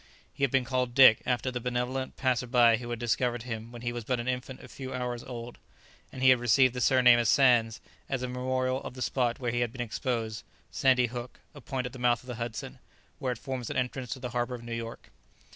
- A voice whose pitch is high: No, low, 125 Hz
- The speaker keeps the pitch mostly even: Yes, narrow, 1.3 semitones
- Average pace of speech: No, fast, 245 wpm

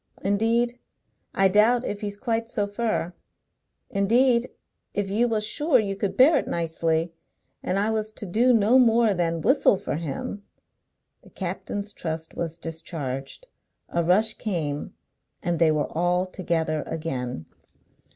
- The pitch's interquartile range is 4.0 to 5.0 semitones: No, wide, 5.4 semitones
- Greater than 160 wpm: No, average, 145 wpm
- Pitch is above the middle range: Yes, high, 200 Hz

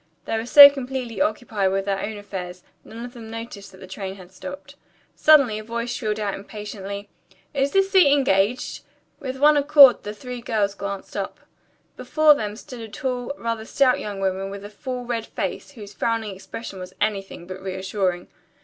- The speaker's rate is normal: Yes, average, 185 wpm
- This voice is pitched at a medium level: No, high, 220 Hz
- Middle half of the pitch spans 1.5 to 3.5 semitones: No, average, 4.2 semitones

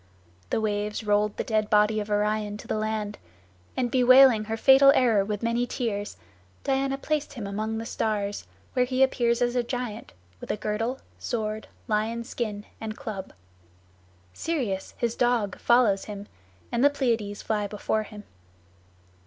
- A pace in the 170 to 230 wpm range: No, average, 155 wpm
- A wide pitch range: No, average, 2.8 semitones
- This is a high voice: Yes, high, 220 Hz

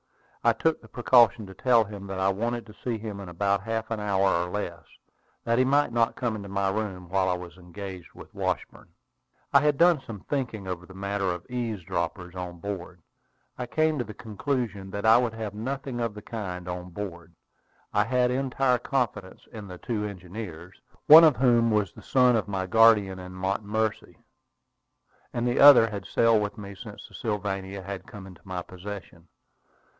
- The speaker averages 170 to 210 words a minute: Yes, average, 190 wpm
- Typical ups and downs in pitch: Yes, average, 3.9 semitones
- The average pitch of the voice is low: Yes, low, 105 Hz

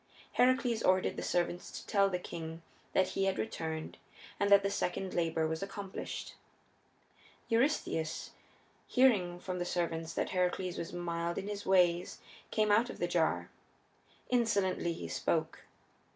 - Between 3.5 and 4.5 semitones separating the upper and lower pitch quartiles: No, average, 3.1 semitones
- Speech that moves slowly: No, average, 145 wpm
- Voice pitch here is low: No, medium, 180 Hz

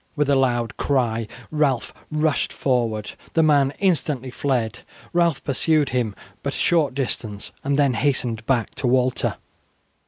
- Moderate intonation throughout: Yes, average, 3.5 semitones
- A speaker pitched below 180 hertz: Yes, low, 135 Hz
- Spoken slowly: No, average, 145 wpm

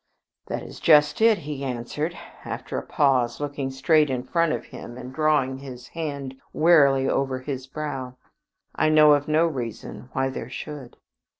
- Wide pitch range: No, average, 2.8 semitones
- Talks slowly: No, average, 165 wpm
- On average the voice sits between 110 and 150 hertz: Yes, medium, 140 Hz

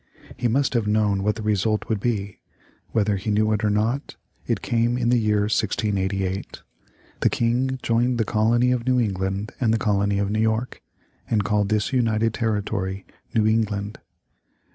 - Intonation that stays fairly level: Yes, narrow, 2.3 semitones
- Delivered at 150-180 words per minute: Yes, average, 170 wpm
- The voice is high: No, low, 110 Hz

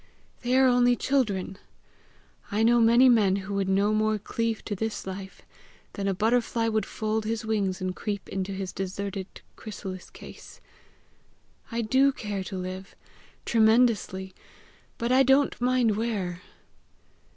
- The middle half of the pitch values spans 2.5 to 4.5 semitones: Yes, average, 3.4 semitones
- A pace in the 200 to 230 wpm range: No, average, 140 wpm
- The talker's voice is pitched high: Yes, high, 215 Hz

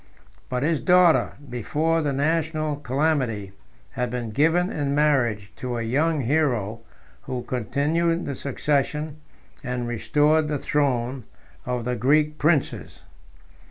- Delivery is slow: Yes, slow, 125 wpm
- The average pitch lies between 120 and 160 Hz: Yes, medium, 140 Hz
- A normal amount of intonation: Yes, average, 3.9 semitones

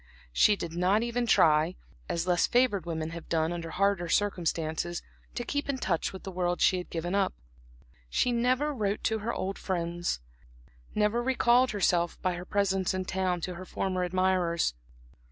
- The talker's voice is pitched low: No, medium, 185 Hz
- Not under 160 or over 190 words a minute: Yes, average, 170 wpm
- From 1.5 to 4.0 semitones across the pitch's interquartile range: Yes, average, 3.4 semitones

